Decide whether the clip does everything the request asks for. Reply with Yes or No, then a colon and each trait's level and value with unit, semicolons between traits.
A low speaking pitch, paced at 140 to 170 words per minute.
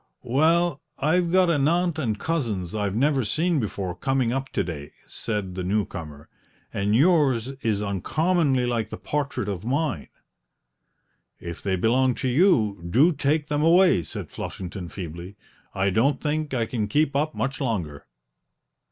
Yes: low, 125 Hz; average, 155 wpm